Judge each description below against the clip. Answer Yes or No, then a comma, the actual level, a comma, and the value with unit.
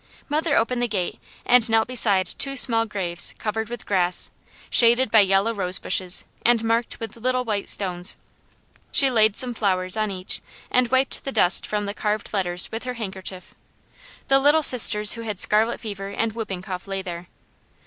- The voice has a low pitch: No, high, 215 Hz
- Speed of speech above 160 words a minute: Yes, average, 180 wpm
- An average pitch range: Yes, average, 3.7 semitones